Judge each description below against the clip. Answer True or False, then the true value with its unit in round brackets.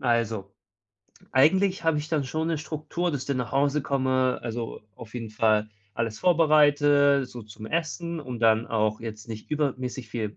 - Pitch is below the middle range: True (130 Hz)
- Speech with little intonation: False (5.0 semitones)